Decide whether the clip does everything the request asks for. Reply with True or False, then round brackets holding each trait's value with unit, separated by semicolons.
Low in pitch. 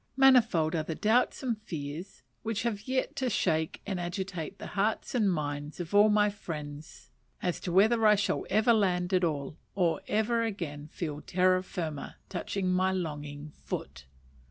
False (185 Hz)